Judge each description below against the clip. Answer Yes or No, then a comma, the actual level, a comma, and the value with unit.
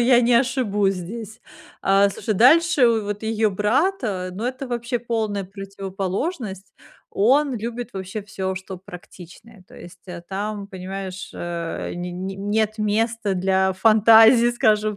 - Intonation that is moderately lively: Yes, average, 3.5 semitones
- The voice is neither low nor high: No, high, 210 Hz